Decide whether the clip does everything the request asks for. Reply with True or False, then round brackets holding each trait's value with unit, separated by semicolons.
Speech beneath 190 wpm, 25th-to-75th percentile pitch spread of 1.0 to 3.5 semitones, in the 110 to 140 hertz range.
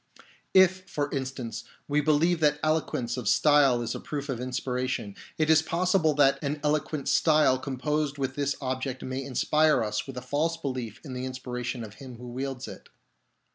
True (175 wpm; 3.2 semitones; 135 Hz)